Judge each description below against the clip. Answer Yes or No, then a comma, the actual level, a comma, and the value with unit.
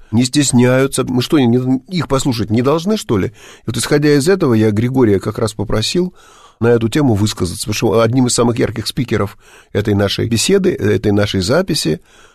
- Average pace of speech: No, fast, 180 wpm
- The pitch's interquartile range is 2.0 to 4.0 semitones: No, average, 5.0 semitones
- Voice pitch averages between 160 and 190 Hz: No, low, 125 Hz